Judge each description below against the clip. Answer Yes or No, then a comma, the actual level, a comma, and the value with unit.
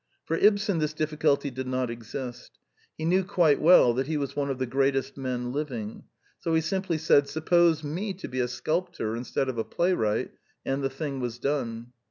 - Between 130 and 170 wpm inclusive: No, average, 200 wpm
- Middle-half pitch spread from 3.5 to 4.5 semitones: Yes, average, 4.2 semitones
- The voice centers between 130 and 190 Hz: Yes, medium, 140 Hz